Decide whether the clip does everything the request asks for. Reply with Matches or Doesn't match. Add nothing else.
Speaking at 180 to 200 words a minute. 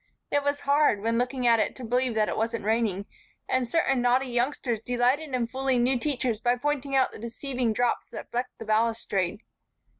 Matches